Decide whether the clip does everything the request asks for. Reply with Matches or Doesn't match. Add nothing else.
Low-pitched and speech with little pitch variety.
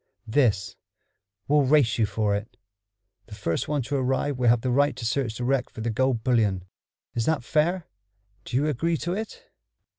Doesn't match